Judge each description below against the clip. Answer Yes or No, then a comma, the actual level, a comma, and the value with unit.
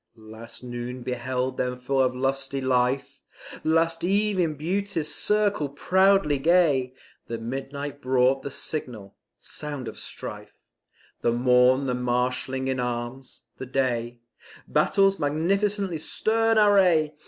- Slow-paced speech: Yes, slow, 120 wpm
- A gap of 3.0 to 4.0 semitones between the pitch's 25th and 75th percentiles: No, average, 4.8 semitones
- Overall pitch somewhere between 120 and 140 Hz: Yes, low, 135 Hz